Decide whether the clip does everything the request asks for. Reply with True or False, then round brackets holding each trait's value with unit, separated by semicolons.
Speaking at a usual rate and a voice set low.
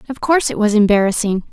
False (195 wpm; 220 Hz)